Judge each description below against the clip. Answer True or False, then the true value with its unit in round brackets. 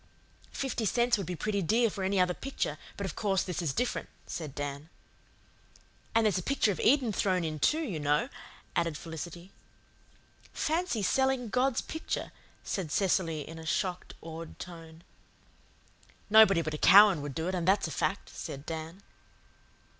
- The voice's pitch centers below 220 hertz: True (185 Hz)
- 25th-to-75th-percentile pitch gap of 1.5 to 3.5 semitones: False (5.2 semitones)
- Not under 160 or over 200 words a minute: True (165 wpm)